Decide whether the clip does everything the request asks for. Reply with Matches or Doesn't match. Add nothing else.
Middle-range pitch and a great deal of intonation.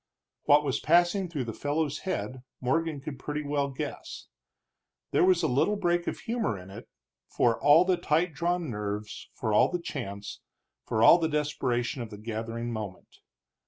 Matches